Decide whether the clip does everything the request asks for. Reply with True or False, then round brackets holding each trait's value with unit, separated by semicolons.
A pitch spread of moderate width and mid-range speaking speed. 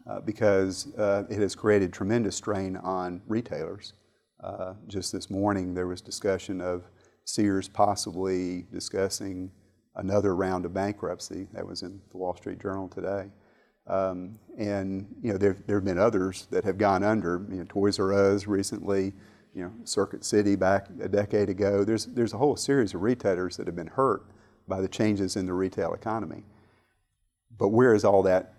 False (1.7 semitones; 175 wpm)